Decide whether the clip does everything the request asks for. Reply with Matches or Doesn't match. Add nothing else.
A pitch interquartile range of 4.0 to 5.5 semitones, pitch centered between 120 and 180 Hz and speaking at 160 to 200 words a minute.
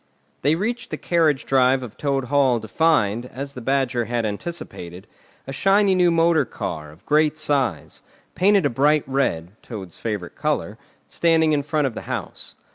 Matches